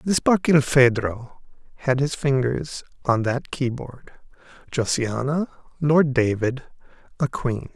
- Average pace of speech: No, slow, 95 wpm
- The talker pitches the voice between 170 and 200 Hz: No, low, 135 Hz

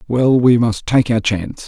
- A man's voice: Yes, male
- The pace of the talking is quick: Yes, fast, 215 wpm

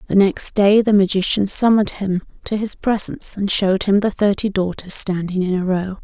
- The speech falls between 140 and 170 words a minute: No, average, 200 wpm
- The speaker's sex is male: No, female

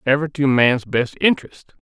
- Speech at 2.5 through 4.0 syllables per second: No, 4.8 syllables/s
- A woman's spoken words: No, male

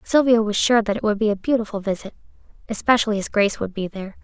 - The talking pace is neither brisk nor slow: No, fast, 225 wpm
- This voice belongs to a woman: Yes, female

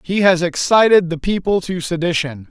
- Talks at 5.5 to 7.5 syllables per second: No, 5.0 syllables/s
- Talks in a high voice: No, medium, 175 Hz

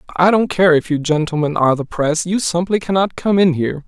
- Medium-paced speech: No, fast, 230 wpm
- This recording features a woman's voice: No, male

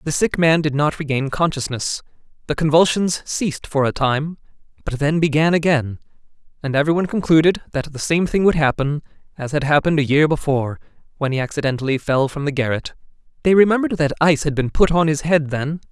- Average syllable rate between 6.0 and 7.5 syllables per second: Yes, 6.2 syllables/s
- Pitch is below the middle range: No, medium, 150 Hz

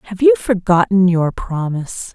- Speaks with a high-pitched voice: Yes, high, 195 Hz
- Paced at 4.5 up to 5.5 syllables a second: Yes, 4.7 syllables/s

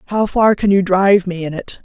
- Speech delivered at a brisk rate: Yes, fast, 260 wpm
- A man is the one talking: No, female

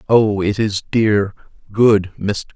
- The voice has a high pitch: No, low, 105 Hz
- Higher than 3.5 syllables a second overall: No, 3.2 syllables/s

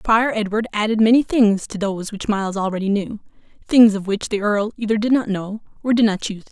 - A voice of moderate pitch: No, high, 210 Hz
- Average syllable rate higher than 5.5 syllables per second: Yes, 6.2 syllables/s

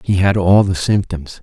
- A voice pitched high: No, very low, 95 Hz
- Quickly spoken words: Yes, fast, 210 wpm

